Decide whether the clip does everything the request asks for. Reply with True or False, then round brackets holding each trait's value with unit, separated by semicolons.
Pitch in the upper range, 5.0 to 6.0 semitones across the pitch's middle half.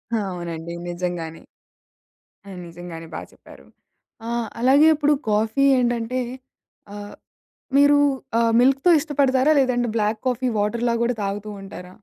True (230 Hz; 5.3 semitones)